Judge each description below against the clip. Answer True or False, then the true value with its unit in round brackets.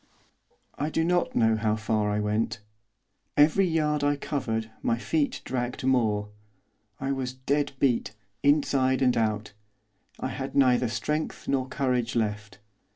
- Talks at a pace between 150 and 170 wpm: False (140 wpm)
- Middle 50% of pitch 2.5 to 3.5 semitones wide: False (4.3 semitones)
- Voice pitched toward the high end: False (130 Hz)